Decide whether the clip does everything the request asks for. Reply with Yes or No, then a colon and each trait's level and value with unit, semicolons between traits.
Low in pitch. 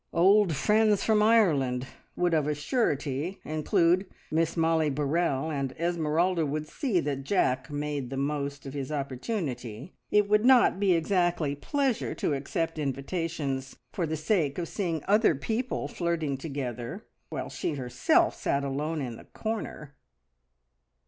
No: medium, 155 Hz